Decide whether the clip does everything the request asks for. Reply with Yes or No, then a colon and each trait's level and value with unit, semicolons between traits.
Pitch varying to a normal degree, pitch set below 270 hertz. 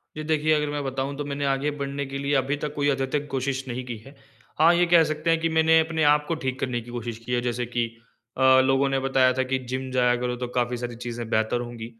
Yes: average, 3.1 semitones; low, 135 Hz